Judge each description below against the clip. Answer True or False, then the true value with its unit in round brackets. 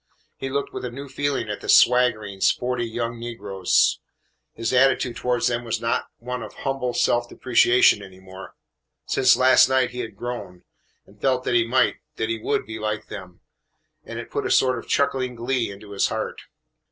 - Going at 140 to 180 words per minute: False (190 wpm)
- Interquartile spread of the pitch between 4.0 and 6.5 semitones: False (2.7 semitones)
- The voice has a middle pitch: False (120 Hz)